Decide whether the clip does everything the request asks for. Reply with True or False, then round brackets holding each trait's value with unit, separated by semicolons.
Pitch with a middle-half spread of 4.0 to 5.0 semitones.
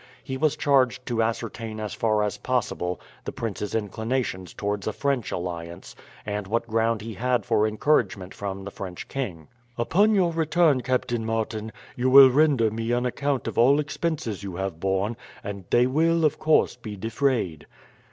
True (4.5 semitones)